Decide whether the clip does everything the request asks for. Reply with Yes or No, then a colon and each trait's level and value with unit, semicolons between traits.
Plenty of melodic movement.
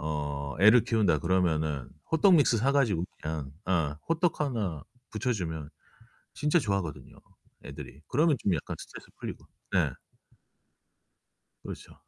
Yes: wide, 8.7 semitones